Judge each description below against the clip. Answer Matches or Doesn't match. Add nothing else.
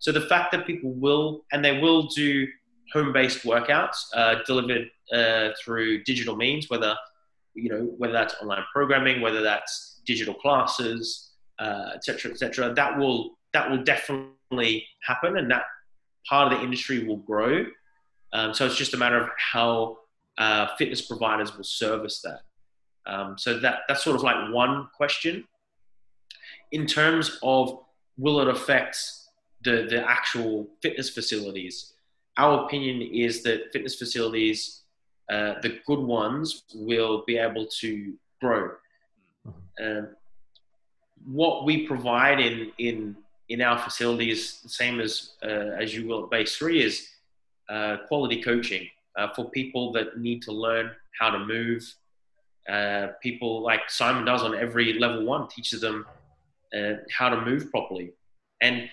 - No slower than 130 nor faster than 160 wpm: Matches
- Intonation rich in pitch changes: Doesn't match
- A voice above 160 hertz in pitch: Doesn't match